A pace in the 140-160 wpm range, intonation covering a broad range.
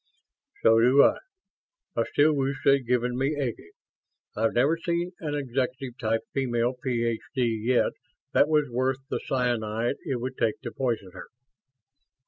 No: average, 145 wpm; average, 2.8 semitones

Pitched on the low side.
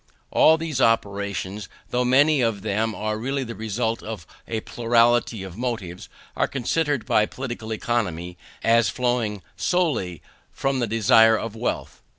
Yes: low, 115 Hz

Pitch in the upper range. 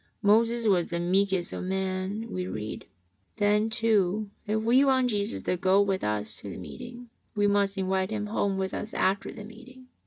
Yes: high, 200 Hz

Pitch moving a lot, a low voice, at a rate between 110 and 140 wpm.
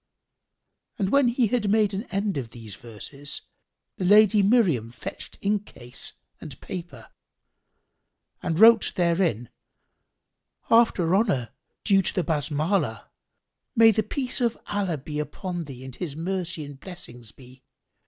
No: wide, 7.1 semitones; medium, 180 Hz; slow, 135 wpm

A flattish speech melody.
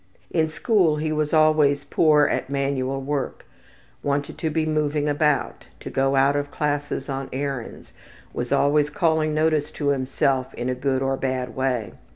Yes: narrow, 2.2 semitones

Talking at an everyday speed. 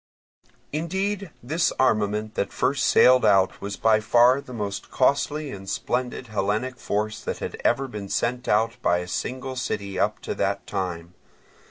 Yes: average, 160 wpm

